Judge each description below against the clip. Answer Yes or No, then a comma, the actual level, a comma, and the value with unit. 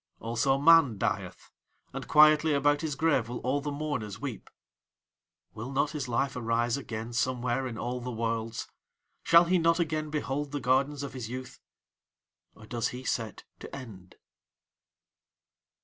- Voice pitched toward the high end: No, low, 130 Hz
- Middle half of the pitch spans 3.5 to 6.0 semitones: Yes, average, 4.0 semitones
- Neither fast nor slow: Yes, average, 150 wpm